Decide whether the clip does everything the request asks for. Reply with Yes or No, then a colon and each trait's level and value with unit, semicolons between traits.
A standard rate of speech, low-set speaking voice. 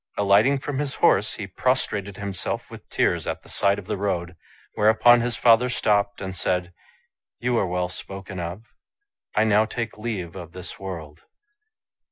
Yes: average, 170 wpm; low, 100 Hz